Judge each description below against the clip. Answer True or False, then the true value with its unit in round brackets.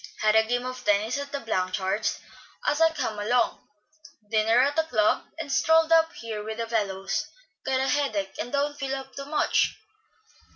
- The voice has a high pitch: True (245 Hz)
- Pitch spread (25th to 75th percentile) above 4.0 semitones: True (4.9 semitones)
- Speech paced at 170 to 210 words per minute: True (180 wpm)